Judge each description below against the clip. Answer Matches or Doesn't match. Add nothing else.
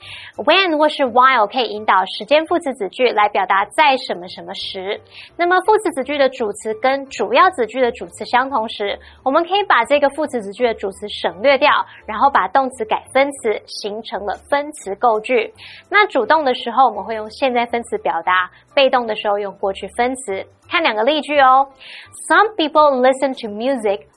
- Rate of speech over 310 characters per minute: Matches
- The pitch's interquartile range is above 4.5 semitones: Matches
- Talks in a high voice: Matches